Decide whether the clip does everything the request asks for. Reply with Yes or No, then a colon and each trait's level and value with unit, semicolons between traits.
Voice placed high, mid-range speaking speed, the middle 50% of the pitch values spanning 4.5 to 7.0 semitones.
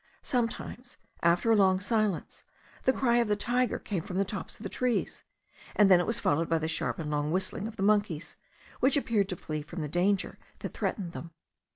No: high, 195 Hz; fast, 210 wpm; average, 5.1 semitones